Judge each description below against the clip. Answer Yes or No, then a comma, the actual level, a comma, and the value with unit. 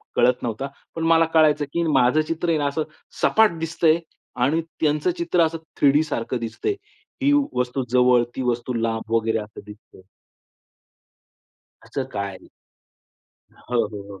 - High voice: No, medium, 140 Hz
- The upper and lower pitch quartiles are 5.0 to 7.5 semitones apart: Yes, wide, 5.5 semitones